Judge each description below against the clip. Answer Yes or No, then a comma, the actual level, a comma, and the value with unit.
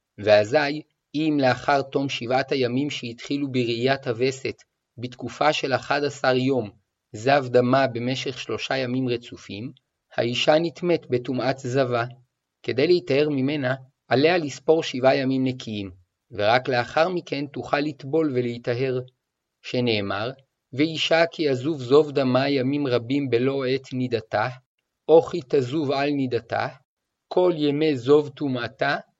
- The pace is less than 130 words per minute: Yes, average, 120 wpm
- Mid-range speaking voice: No, low, 130 Hz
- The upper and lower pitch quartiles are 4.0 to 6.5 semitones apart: No, average, 2.8 semitones